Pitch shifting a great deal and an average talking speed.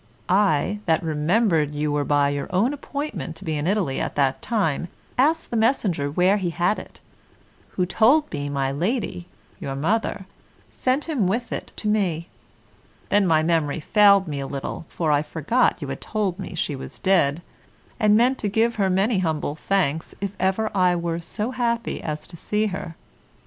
Yes: wide, 5.9 semitones; average, 180 wpm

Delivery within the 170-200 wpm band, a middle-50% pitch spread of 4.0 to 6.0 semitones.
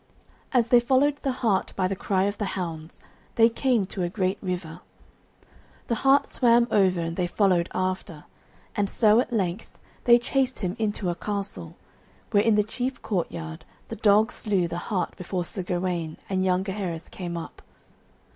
Yes: average, 175 wpm; average, 4.3 semitones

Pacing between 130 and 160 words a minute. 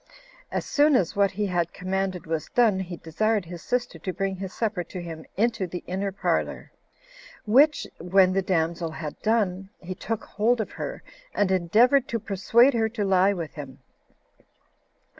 No: average, 170 wpm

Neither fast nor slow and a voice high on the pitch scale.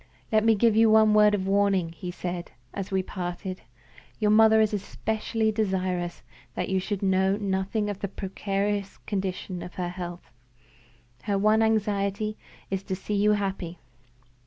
Yes: average, 160 wpm; high, 200 Hz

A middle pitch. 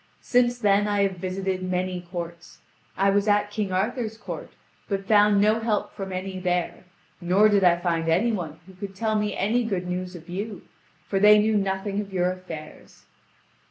No: high, 195 Hz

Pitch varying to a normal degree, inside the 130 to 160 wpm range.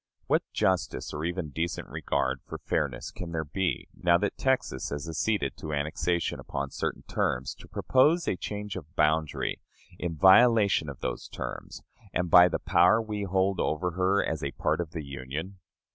No: average, 3.9 semitones; average, 175 wpm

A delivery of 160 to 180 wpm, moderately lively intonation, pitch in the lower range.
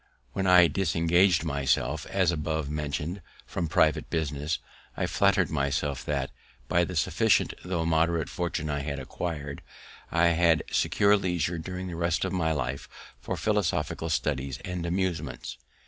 No: average, 145 wpm; average, 3.1 semitones; very low, 80 Hz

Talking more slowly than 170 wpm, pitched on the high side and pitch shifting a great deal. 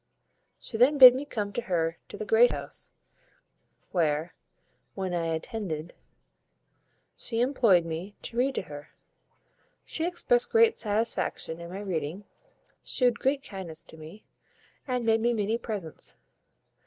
Yes: average, 140 wpm; high, 210 Hz; wide, 6.5 semitones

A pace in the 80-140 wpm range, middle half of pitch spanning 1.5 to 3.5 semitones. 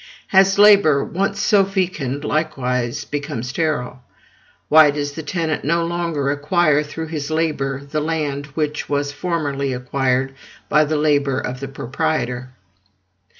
Yes: slow, 135 wpm; average, 2.8 semitones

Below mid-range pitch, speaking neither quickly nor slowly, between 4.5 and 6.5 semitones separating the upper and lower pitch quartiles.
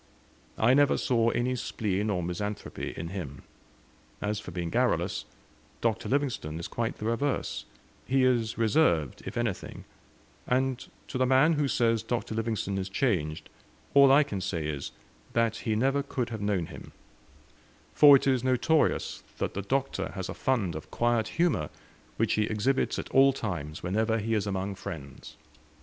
Yes: low, 115 Hz; average, 165 wpm; average, 5.0 semitones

